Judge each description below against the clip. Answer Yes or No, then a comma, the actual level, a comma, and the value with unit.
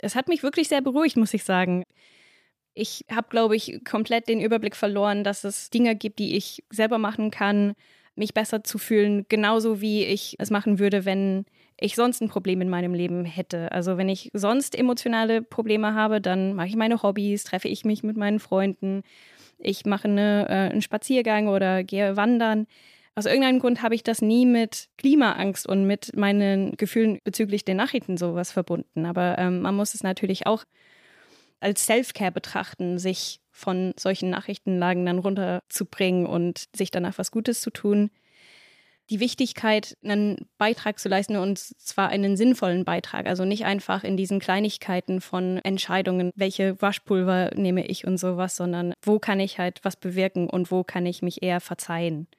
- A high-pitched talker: Yes, high, 200 Hz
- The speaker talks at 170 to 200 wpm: Yes, average, 175 wpm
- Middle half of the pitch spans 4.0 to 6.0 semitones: No, average, 2.7 semitones